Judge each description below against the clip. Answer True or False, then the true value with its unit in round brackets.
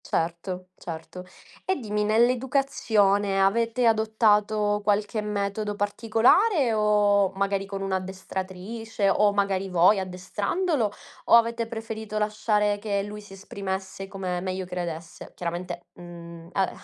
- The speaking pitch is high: True (205 Hz)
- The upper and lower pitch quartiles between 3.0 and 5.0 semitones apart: False (2.5 semitones)